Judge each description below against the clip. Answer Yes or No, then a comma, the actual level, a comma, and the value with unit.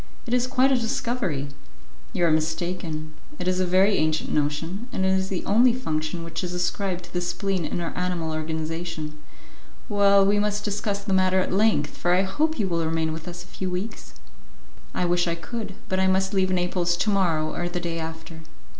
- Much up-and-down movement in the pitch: No, average, 3.3 semitones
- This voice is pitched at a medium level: Yes, medium, 180 Hz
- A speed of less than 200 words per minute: No, fast, 205 wpm